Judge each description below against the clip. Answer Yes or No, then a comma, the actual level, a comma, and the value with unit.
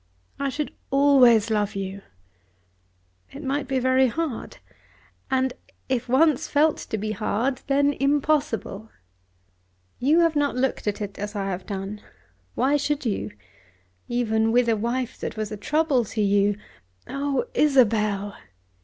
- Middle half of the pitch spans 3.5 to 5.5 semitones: Yes, average, 5.0 semitones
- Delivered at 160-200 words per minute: No, average, 145 wpm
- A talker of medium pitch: No, high, 245 Hz